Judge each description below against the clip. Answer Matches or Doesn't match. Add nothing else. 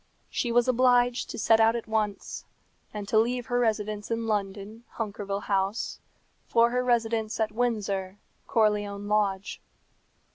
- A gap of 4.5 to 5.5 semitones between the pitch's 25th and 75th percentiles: Doesn't match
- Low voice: Doesn't match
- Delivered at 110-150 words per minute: Matches